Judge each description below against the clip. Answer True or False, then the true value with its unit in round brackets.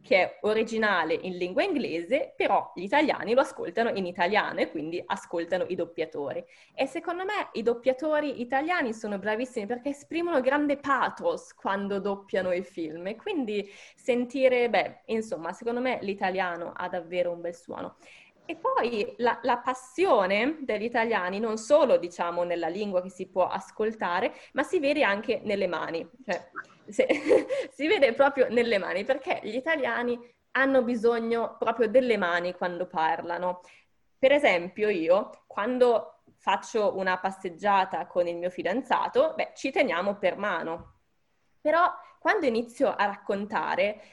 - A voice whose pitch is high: True (230 Hz)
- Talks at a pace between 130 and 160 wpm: True (145 wpm)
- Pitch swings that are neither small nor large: False (6.6 semitones)